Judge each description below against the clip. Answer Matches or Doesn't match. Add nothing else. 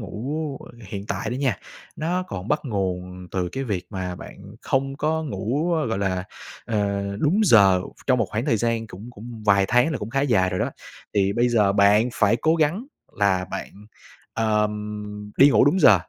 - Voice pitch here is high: Doesn't match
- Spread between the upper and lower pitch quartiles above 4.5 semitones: Matches